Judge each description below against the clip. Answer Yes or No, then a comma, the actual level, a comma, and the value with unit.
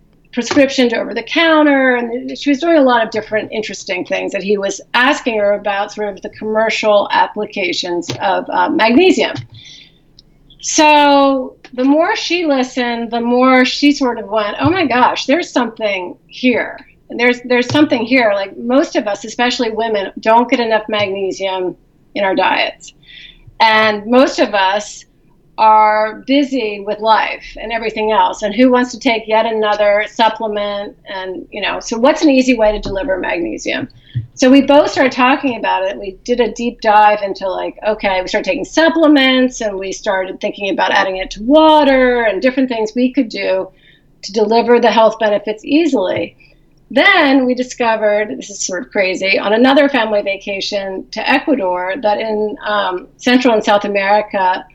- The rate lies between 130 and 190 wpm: Yes, average, 170 wpm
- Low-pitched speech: No, high, 225 Hz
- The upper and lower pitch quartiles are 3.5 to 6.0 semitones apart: Yes, average, 4.5 semitones